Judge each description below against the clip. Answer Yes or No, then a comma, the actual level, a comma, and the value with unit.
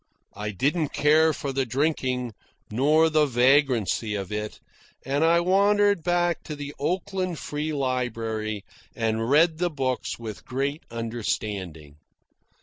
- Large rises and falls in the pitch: Yes, wide, 5.8 semitones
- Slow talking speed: Yes, slow, 130 wpm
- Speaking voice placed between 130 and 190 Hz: Yes, low, 135 Hz